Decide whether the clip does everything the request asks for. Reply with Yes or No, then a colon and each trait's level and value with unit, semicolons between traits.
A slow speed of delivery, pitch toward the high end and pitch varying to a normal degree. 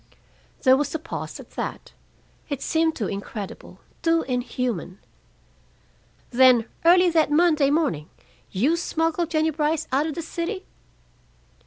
Yes: slow, 130 wpm; very high, 305 Hz; average, 4.6 semitones